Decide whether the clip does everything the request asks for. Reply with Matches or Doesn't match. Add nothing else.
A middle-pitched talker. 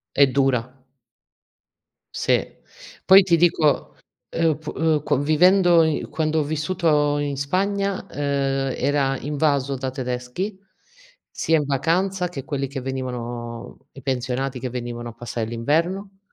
Matches